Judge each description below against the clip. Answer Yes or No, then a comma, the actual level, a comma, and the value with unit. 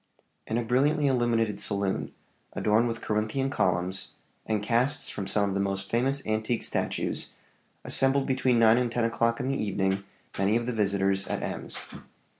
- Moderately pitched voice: No, low, 115 Hz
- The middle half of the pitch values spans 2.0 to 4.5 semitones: Yes, average, 3.8 semitones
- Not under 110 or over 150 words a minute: No, average, 165 wpm